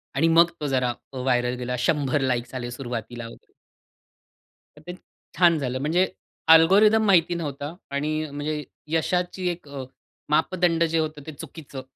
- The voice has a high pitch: No, medium, 150 Hz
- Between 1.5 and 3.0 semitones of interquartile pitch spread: No, average, 4.4 semitones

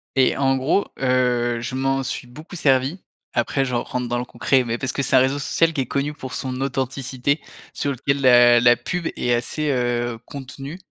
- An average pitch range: No, narrow, 2.2 semitones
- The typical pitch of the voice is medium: No, low, 130 Hz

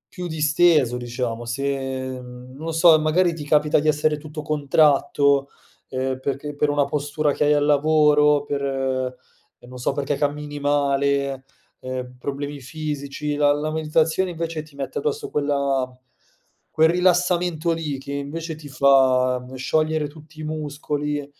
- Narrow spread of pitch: Yes, narrow, 2.1 semitones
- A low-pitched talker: No, medium, 145 Hz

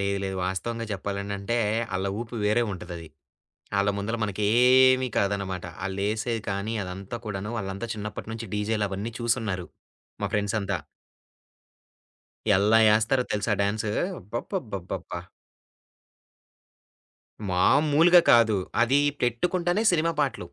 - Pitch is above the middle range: No, low, 105 Hz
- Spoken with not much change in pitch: No, average, 3.2 semitones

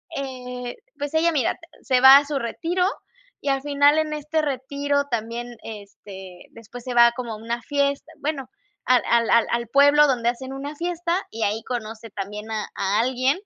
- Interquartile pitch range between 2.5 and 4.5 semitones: Yes, average, 3.7 semitones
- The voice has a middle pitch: No, very high, 255 Hz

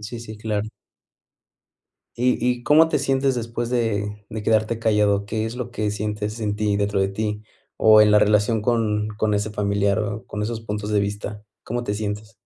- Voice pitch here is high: No, low, 105 Hz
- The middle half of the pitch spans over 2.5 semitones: No, narrow, 1.7 semitones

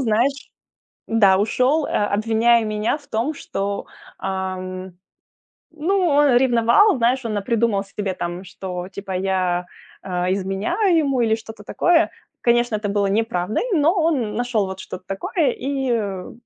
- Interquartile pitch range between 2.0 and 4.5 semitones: No, average, 5.1 semitones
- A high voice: Yes, high, 220 Hz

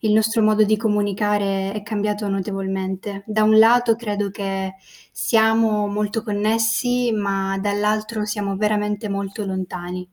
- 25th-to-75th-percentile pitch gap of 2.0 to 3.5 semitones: No, narrow, 1.6 semitones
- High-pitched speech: Yes, high, 210 Hz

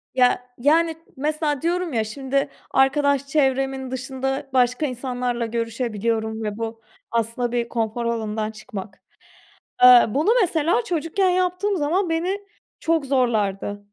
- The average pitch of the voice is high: Yes, very high, 260 Hz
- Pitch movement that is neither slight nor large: Yes, average, 5.0 semitones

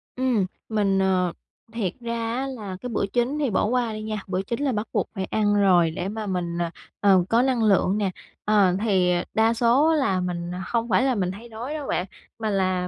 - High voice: Yes, high, 210 Hz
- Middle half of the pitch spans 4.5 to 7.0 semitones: No, average, 4.0 semitones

